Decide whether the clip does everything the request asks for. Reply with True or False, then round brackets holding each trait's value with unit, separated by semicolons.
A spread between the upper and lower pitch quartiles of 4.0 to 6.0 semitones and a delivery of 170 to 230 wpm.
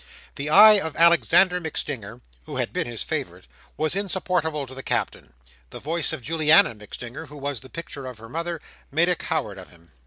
True (5.0 semitones; 190 wpm)